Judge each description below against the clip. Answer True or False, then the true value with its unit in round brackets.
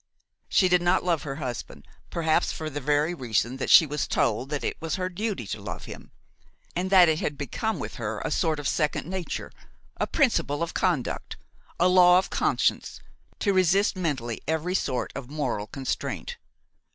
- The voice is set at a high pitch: False (155 Hz)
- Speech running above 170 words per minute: True (180 wpm)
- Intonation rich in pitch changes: False (4.8 semitones)